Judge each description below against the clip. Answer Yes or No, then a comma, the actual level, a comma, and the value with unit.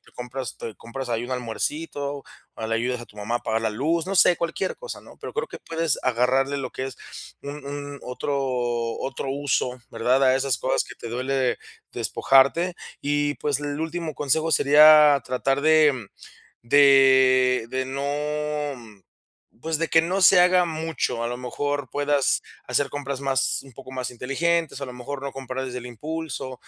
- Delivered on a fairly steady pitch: No, average, 3.0 semitones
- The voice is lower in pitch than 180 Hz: Yes, low, 135 Hz